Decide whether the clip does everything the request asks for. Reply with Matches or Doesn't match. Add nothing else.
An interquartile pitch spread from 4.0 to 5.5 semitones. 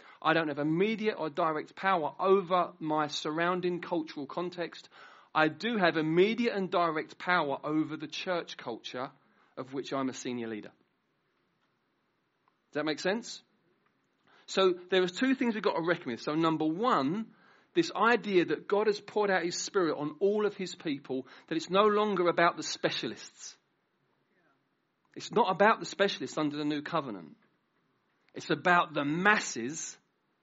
Matches